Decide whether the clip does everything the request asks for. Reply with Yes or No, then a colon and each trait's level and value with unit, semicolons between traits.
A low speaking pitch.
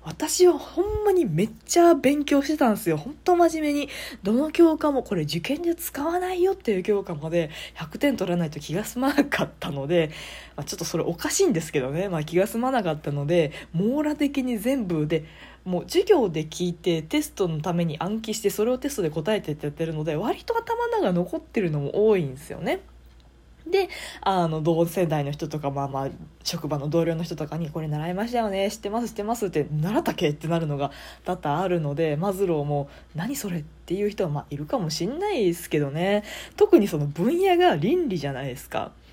No: high, 190 Hz